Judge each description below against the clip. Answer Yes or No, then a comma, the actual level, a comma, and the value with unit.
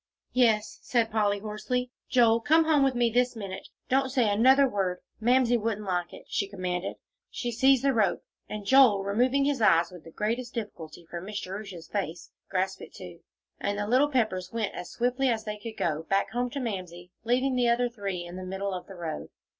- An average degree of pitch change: Yes, average, 4.4 semitones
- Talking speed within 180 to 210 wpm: Yes, average, 200 wpm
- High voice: Yes, high, 215 Hz